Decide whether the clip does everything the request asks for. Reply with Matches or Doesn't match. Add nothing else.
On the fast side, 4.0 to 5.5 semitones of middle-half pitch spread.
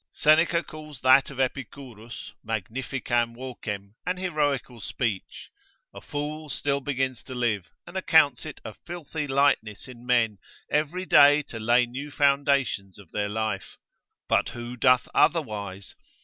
Doesn't match